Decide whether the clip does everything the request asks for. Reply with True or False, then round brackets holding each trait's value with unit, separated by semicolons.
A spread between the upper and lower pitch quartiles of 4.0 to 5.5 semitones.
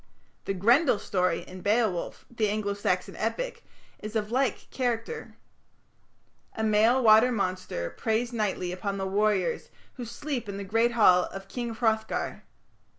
False (3.3 semitones)